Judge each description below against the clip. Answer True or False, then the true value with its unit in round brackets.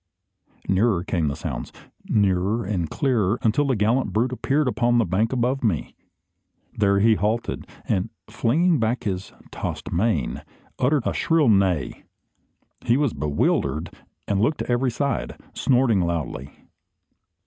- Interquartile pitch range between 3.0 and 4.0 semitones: False (5.3 semitones)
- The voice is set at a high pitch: False (110 Hz)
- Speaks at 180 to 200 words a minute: False (135 wpm)